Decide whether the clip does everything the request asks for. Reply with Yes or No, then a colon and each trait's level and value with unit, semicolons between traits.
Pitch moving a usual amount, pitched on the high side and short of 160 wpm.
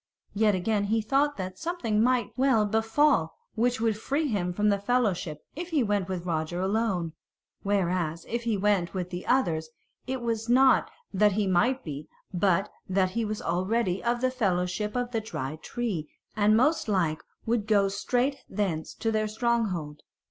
No: average, 4.5 semitones; high, 210 Hz; average, 170 wpm